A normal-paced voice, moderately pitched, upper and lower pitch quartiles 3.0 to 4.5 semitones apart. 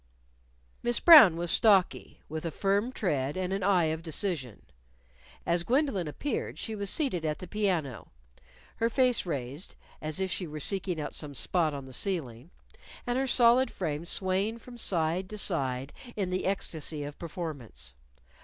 No: average, 165 wpm; medium, 180 Hz; average, 5.0 semitones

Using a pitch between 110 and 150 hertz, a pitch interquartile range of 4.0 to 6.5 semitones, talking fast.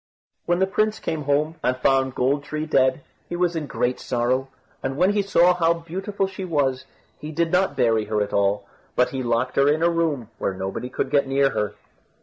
Yes: medium, 140 Hz; average, 4.9 semitones; fast, 210 wpm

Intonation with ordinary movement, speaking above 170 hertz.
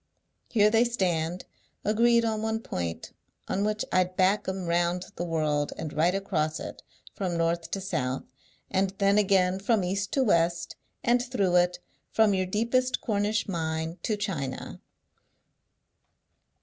Yes: average, 3.9 semitones; high, 190 Hz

